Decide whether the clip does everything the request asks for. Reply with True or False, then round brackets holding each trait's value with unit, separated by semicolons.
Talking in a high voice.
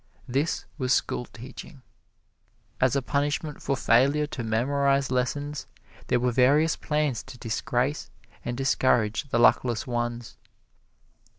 False (130 Hz)